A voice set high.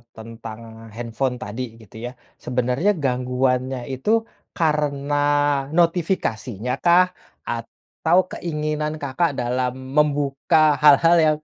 No: low, 135 Hz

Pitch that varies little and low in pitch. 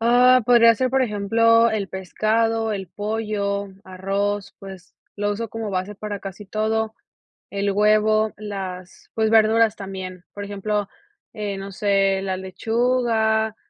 No: narrow, 2.2 semitones; high, 210 Hz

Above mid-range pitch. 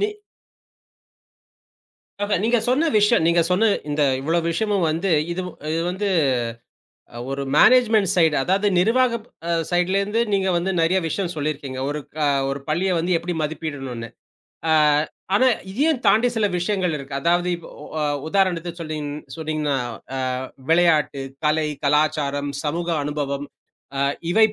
No: medium, 170 Hz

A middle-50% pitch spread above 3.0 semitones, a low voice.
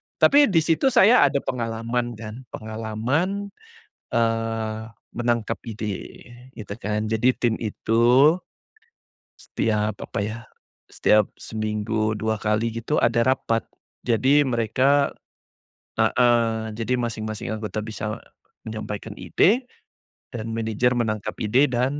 No: narrow, 2.5 semitones; low, 115 Hz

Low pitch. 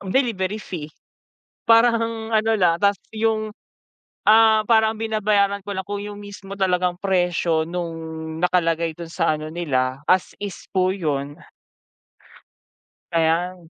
No: high, 190 Hz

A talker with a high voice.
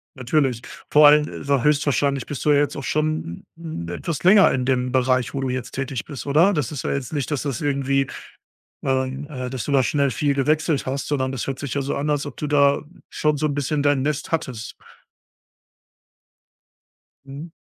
No: medium, 140 Hz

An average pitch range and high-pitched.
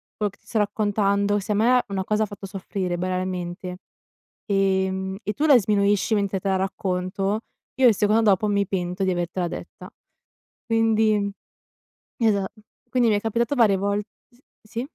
No: narrow, 2.3 semitones; high, 200 Hz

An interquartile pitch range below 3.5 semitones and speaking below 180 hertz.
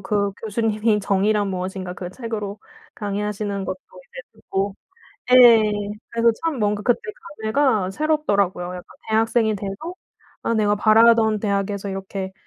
No: narrow, 2.5 semitones; high, 210 Hz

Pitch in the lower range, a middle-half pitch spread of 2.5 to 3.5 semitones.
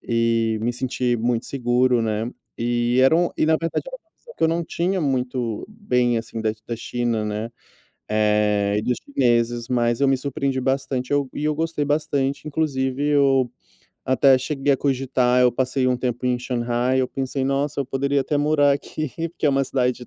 Yes: low, 130 Hz; average, 2.8 semitones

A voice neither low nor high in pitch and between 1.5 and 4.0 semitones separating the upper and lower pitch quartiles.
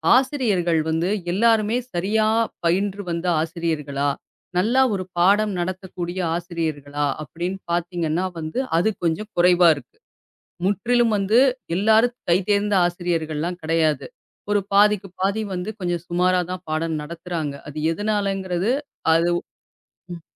Yes: medium, 180 Hz; average, 3.5 semitones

